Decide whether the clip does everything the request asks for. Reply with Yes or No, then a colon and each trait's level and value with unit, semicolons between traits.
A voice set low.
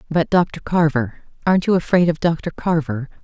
No: medium, 160 Hz